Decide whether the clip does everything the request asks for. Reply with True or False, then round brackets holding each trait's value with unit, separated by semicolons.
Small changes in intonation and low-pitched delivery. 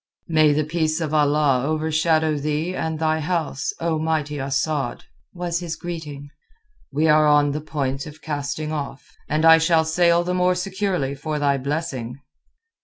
False (2.0 semitones; 155 Hz)